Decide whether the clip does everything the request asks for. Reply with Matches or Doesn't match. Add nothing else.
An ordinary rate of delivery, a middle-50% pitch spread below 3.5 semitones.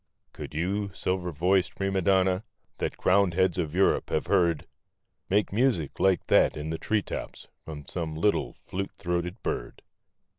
Matches